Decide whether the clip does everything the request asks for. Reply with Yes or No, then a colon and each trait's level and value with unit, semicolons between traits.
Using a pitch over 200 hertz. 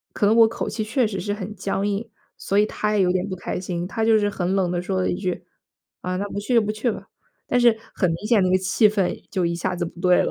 No: high, 195 Hz